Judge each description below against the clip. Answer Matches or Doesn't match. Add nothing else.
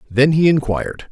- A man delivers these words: Matches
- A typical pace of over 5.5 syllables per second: Doesn't match